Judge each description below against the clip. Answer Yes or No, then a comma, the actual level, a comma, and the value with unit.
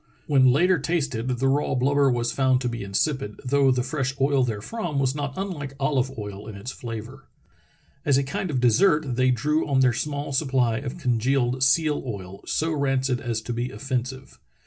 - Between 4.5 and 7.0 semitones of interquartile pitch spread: No, average, 2.7 semitones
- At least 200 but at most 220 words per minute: No, average, 185 wpm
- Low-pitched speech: Yes, low, 130 Hz